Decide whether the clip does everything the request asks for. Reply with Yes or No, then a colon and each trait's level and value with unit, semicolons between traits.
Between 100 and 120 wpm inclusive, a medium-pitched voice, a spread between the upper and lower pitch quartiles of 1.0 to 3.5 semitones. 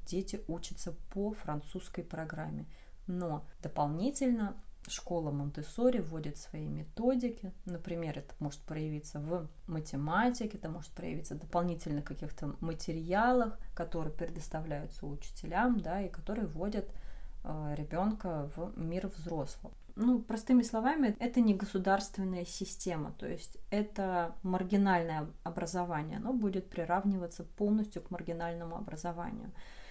No: slow, 110 wpm; medium, 175 Hz; average, 4.3 semitones